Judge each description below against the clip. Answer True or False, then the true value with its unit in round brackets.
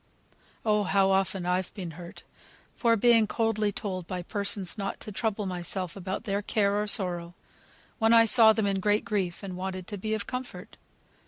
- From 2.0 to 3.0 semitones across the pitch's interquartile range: True (2.7 semitones)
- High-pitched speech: True (200 Hz)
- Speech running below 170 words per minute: False (180 wpm)